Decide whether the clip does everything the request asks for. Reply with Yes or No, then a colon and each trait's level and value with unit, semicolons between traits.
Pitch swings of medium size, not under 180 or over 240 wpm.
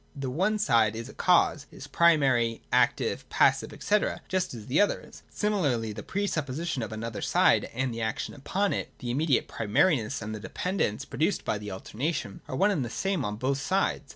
No: wide, 7.7 semitones; average, 200 wpm